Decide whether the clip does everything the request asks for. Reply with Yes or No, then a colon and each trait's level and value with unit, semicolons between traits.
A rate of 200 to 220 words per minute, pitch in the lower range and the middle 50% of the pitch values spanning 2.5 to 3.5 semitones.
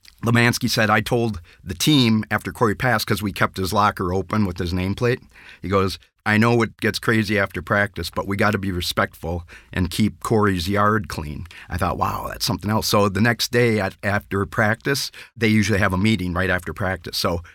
Yes: fast, 205 wpm; low, 105 Hz; average, 3.0 semitones